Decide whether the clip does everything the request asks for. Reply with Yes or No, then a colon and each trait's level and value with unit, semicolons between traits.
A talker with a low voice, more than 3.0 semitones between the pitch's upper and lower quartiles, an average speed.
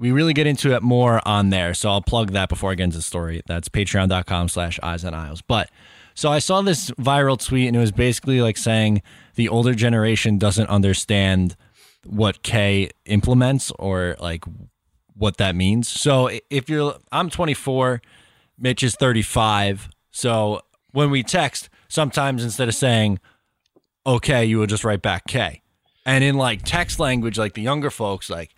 Yes: low, 110 Hz; average, 4.7 semitones; average, 175 wpm